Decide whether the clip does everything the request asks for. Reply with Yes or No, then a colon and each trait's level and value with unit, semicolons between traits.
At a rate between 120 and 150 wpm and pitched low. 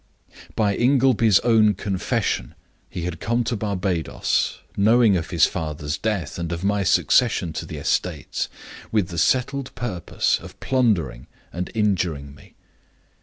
Yes: slow, 135 wpm; low, 100 Hz